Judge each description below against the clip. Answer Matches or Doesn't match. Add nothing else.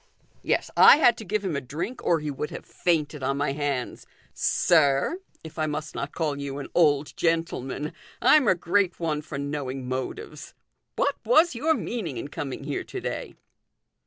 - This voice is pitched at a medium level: Matches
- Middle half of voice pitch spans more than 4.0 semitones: Matches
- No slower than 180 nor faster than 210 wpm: Matches